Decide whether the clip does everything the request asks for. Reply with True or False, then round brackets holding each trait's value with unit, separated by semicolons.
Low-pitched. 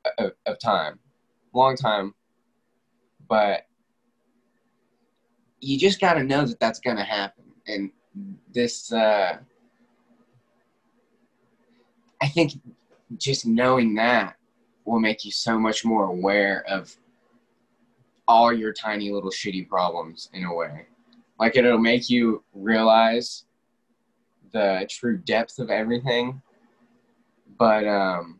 True (115 Hz)